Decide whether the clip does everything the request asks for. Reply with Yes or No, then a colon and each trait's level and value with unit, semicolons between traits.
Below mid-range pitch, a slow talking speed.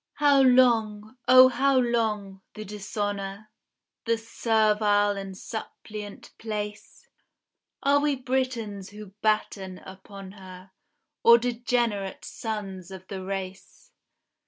No: high, 210 Hz; slow, 105 wpm